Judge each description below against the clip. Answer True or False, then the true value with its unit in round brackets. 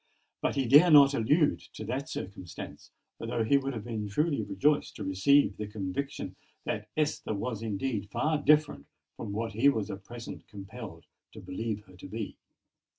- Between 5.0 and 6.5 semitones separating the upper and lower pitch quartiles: True (5.6 semitones)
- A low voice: True (115 Hz)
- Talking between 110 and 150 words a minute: False (170 wpm)